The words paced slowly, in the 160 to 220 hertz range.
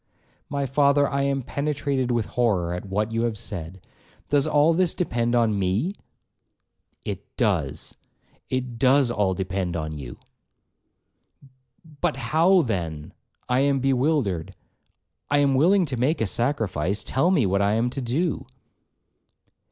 No: slow, 125 wpm; low, 125 Hz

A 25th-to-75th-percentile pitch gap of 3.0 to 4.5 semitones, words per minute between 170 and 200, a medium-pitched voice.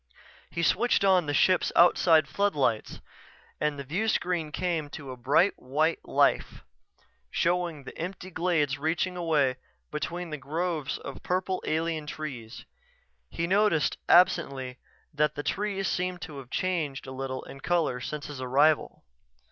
No: average, 4.2 semitones; slow, 135 wpm; medium, 160 Hz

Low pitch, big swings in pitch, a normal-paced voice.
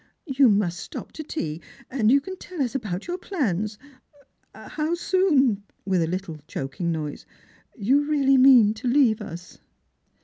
No: high, 240 Hz; wide, 7.3 semitones; average, 160 wpm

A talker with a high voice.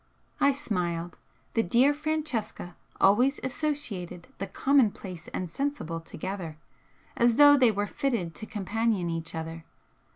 Yes: high, 210 Hz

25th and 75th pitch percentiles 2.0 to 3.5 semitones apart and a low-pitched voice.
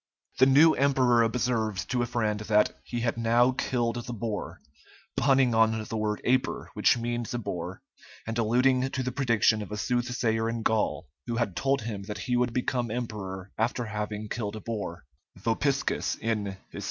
Yes: narrow, 2.4 semitones; low, 115 Hz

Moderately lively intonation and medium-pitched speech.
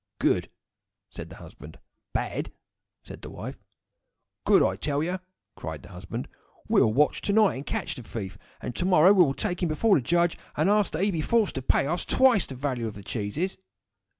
No: wide, 8.1 semitones; medium, 155 Hz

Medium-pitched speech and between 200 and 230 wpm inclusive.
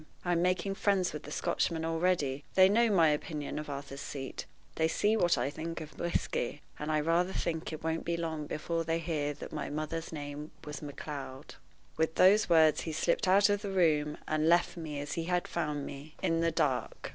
Yes: medium, 160 Hz; fast, 205 wpm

